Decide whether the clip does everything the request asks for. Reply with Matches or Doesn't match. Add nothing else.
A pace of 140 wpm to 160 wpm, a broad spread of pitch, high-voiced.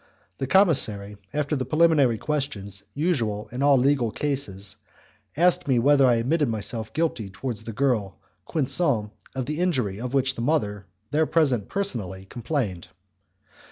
Doesn't match